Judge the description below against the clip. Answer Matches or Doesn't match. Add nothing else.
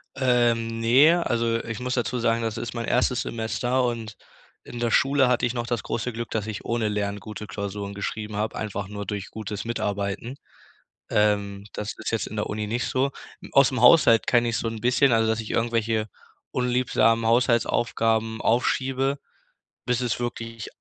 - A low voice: Matches